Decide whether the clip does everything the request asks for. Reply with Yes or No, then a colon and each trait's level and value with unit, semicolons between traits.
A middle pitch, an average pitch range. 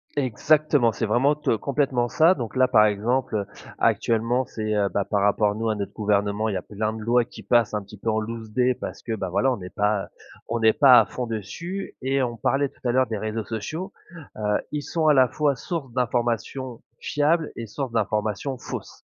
No: low, 115 Hz; average, 3.7 semitones